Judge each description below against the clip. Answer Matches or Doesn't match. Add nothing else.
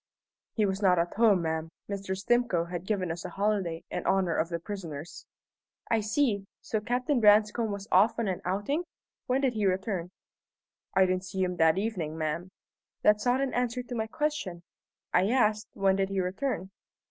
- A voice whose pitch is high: Matches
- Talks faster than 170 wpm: Matches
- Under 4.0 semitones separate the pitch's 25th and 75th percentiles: Matches